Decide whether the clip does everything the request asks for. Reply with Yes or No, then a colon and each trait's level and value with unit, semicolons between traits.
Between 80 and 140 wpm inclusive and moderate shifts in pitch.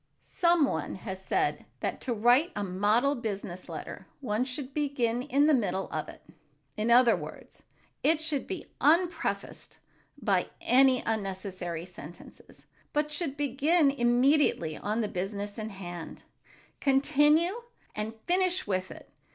No: slow, 135 wpm; wide, 6.6 semitones